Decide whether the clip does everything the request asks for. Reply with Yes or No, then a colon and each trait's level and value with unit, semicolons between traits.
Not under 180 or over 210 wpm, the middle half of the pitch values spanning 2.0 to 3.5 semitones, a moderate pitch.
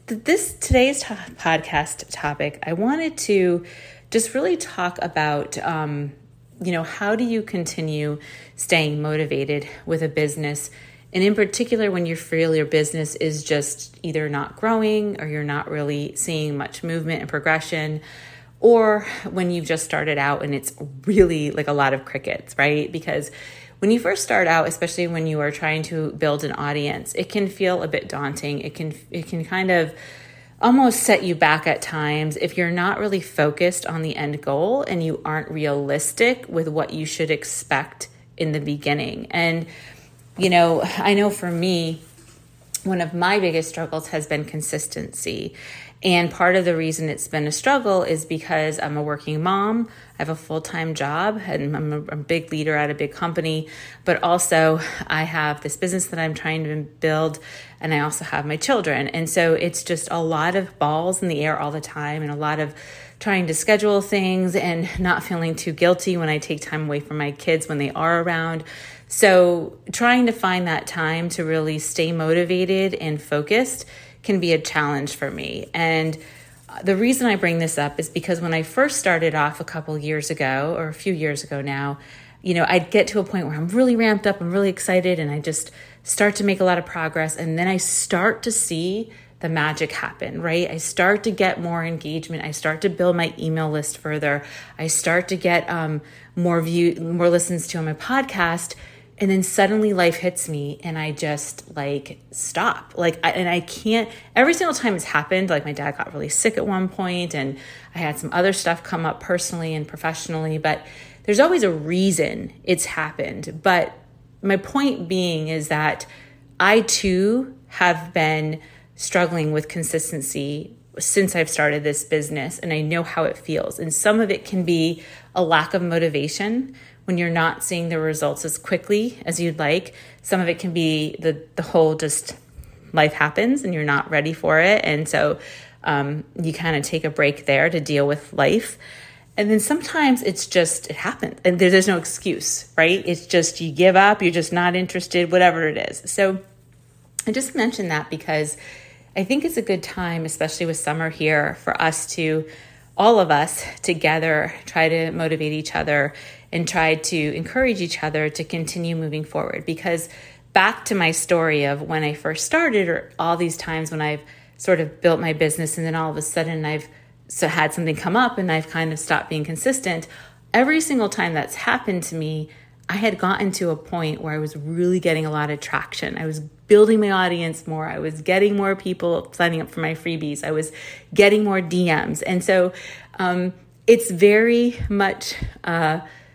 Yes: average, 190 wpm; average, 3.2 semitones; medium, 165 Hz